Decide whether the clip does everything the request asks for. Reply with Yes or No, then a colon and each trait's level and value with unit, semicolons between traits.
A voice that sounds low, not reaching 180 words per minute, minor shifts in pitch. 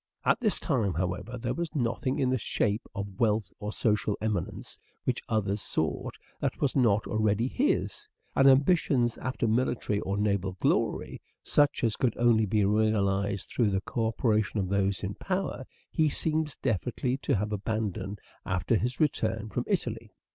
No: low, 110 Hz; average, 160 wpm; average, 4.2 semitones